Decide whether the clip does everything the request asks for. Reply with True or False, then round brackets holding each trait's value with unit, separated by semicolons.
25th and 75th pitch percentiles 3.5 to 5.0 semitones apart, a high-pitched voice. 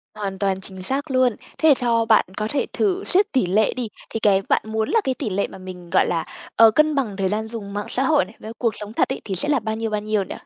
True (4.6 semitones; 220 Hz)